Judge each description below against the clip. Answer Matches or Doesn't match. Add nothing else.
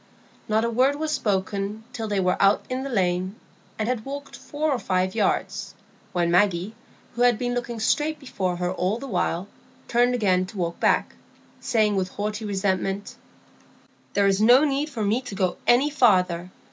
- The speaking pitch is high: Matches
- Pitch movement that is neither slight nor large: Matches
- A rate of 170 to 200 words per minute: Matches